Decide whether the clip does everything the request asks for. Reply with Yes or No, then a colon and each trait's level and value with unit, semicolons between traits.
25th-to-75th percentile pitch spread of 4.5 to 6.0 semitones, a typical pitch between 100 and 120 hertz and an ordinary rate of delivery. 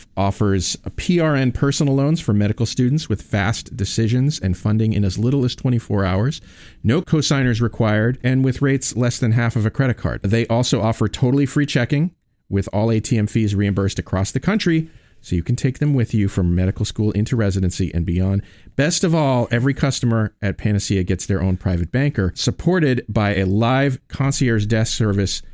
Yes: average, 5.2 semitones; low, 115 Hz; average, 185 wpm